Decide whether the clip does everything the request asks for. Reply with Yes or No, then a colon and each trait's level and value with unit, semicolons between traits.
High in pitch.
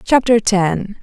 Yes: high, 210 Hz